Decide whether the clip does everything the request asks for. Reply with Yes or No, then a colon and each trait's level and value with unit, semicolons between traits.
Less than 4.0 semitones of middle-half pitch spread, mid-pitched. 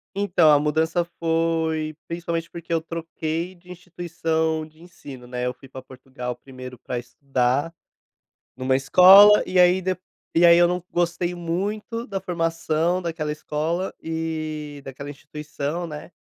Yes: average, 2.9 semitones; medium, 165 Hz